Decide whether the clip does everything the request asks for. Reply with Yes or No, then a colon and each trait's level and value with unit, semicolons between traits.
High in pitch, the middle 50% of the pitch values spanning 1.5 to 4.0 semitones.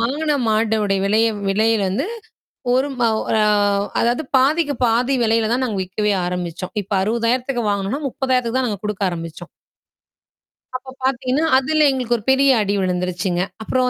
No: high, 230 Hz; average, 4.5 semitones